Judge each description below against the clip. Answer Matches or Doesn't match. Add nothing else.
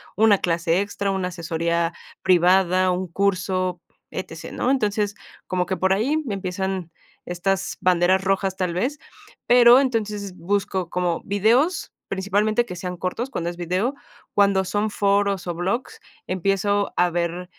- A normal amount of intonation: Doesn't match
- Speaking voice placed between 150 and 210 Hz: Matches